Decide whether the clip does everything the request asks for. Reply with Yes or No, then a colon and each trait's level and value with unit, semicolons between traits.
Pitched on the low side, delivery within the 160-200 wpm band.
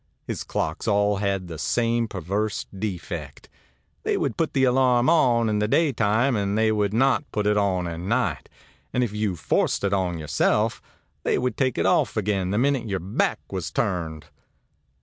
Yes: low, 105 Hz; average, 180 wpm